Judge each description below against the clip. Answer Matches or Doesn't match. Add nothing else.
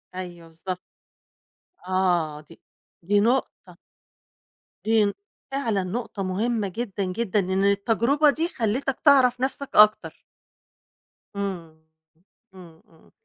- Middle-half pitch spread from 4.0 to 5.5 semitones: Matches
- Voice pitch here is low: Doesn't match